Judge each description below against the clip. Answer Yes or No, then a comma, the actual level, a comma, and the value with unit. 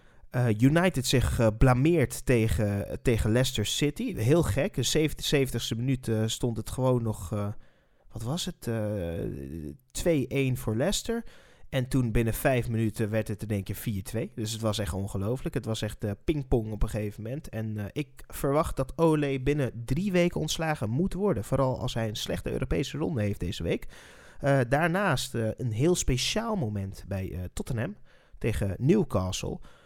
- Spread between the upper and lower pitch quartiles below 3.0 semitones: No, average, 4.5 semitones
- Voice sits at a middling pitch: No, low, 120 Hz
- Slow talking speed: No, average, 175 wpm